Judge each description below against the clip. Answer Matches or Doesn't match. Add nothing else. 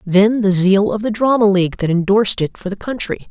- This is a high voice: Matches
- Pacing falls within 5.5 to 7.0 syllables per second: Matches